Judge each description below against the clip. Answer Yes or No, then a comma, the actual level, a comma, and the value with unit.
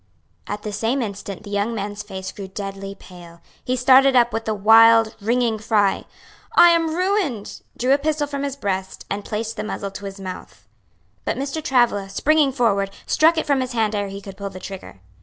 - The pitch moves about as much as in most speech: Yes, average, 5.0 semitones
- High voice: Yes, high, 220 Hz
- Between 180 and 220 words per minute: Yes, average, 200 wpm